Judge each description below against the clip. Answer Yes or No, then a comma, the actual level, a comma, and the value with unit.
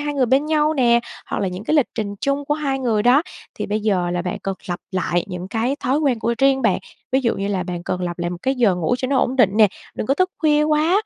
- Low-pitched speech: No, high, 240 Hz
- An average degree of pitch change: No, wide, 6.5 semitones